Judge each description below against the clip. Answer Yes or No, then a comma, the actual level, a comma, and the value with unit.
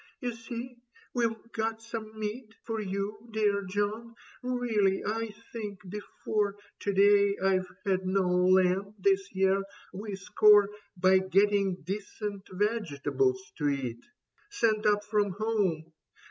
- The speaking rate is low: Yes, slow, 130 wpm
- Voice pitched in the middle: No, high, 205 Hz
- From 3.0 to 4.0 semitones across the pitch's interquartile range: No, narrow, 2.5 semitones